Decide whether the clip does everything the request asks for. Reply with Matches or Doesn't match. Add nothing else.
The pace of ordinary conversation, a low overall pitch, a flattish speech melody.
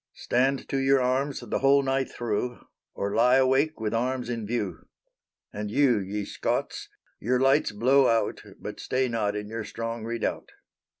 Doesn't match